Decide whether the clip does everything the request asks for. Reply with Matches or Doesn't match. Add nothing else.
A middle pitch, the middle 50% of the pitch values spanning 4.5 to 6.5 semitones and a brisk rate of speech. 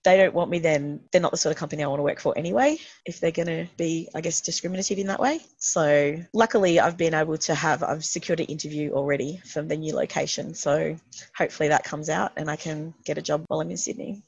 Doesn't match